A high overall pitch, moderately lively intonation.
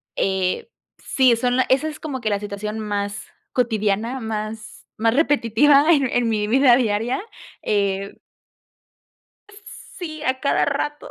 Yes: high, 230 Hz; average, 4.3 semitones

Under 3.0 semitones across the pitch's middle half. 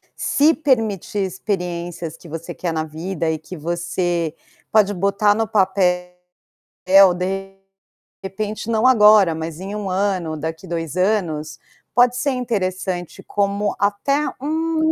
No: average, 3.8 semitones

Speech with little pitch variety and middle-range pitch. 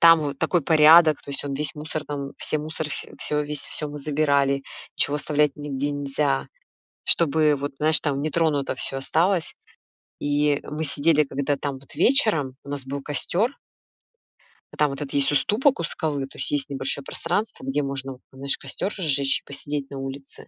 Yes: narrow, 1.9 semitones; medium, 145 Hz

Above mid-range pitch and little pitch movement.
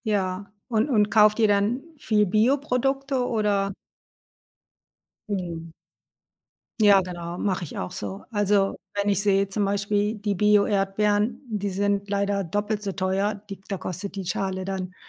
Yes: high, 200 Hz; narrow, 1.6 semitones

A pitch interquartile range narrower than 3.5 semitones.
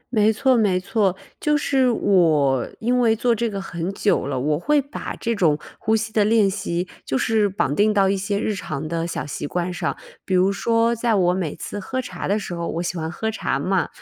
No: average, 4.3 semitones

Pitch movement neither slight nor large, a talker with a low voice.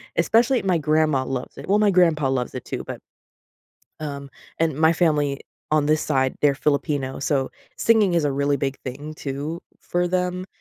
No: average, 4.0 semitones; medium, 150 Hz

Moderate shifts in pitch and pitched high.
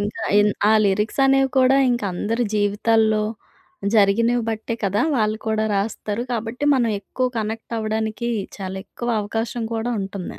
No: narrow, 2.2 semitones; high, 220 Hz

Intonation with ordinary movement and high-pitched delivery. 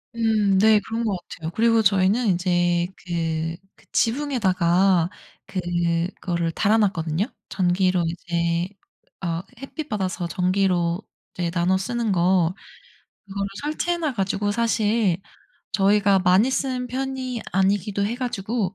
Yes: average, 4.2 semitones; high, 195 Hz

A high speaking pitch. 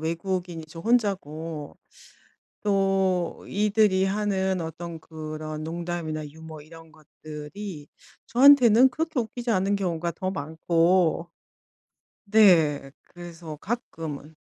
No: medium, 175 Hz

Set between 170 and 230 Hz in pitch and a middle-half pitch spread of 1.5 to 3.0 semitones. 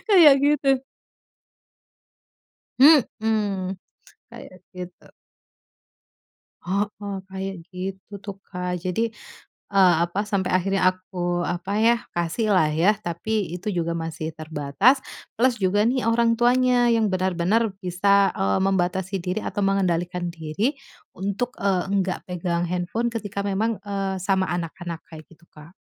No: high, 190 Hz; average, 3.4 semitones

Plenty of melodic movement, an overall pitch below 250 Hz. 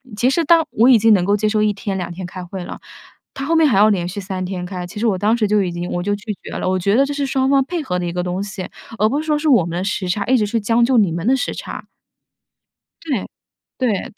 Yes: wide, 5.7 semitones; high, 210 Hz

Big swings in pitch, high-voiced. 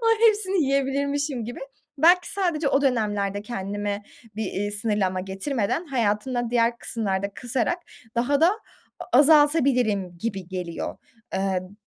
Yes: wide, 5.9 semitones; high, 235 Hz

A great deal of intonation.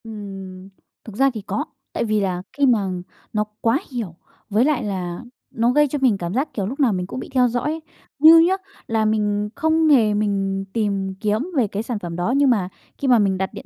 No: average, 4.7 semitones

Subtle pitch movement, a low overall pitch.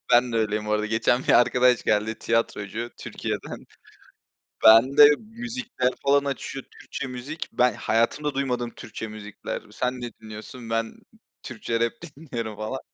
No: average, 3.4 semitones; low, 120 Hz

